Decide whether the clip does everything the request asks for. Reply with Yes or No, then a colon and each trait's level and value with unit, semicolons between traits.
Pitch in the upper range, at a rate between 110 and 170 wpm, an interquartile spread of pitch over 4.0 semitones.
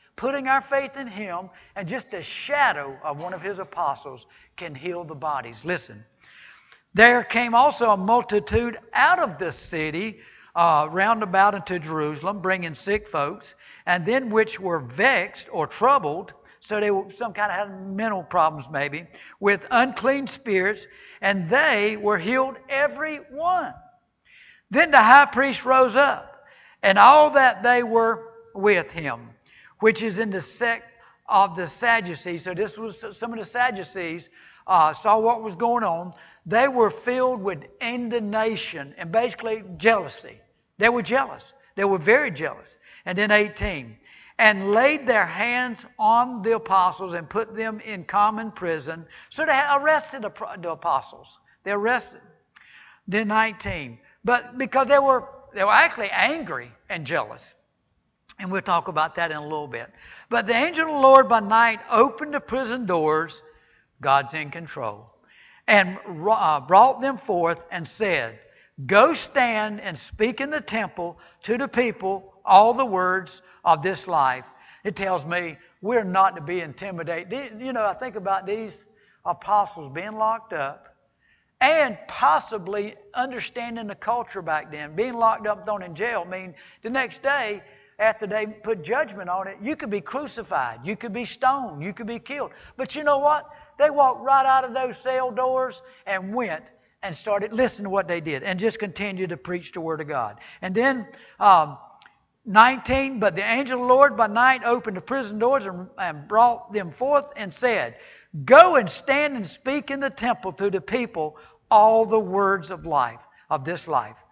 Yes: high, 210 Hz; average, 165 wpm; average, 5.2 semitones